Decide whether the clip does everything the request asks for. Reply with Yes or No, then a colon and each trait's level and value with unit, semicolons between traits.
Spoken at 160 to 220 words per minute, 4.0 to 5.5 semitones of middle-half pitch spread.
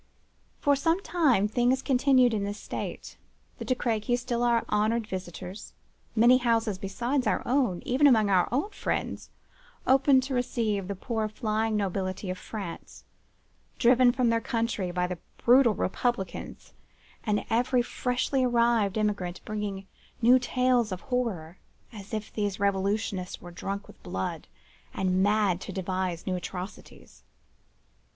No: slow, 135 wpm; average, 4.3 semitones